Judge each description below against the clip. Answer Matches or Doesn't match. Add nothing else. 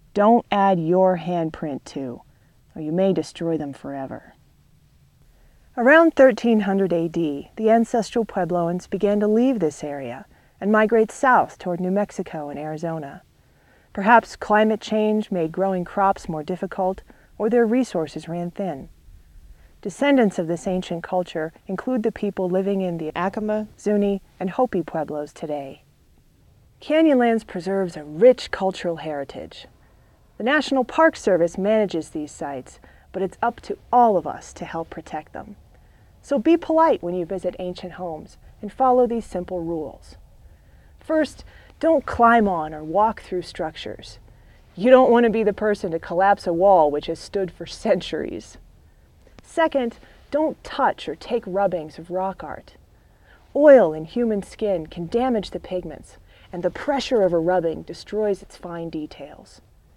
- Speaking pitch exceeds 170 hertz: Matches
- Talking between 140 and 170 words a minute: Matches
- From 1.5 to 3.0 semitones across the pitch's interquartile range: Doesn't match